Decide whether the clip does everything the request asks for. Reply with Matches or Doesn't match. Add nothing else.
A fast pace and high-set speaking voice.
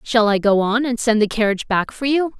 Matches